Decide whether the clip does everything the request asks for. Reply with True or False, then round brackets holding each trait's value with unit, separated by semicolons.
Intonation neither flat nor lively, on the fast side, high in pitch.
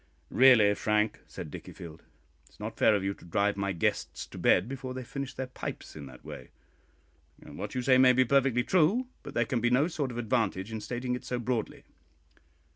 False (4.0 semitones; 210 wpm; 120 Hz)